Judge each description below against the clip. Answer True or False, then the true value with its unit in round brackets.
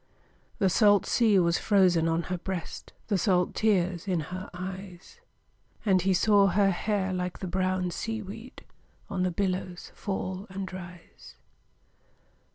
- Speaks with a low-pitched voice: False (185 Hz)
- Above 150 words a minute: False (145 wpm)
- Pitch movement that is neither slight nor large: False (1.8 semitones)